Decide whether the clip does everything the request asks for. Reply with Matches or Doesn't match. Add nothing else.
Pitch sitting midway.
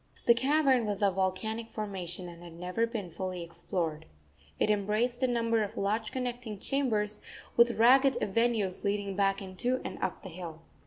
Doesn't match